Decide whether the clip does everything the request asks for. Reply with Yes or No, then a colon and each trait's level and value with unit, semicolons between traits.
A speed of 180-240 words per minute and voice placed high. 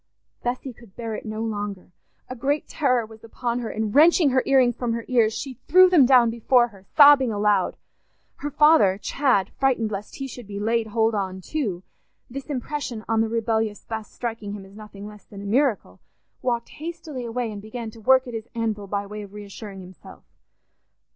Yes: average, 195 wpm; high, 230 Hz